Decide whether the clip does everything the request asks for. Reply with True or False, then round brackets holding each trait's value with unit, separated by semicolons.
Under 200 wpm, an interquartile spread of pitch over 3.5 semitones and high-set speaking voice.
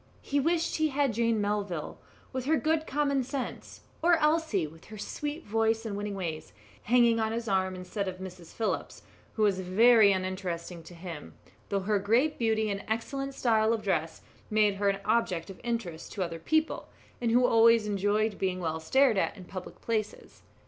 True (185 wpm; 4.4 semitones; 215 Hz)